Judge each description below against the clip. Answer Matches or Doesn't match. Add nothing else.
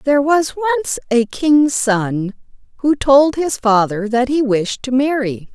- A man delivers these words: Doesn't match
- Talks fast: Doesn't match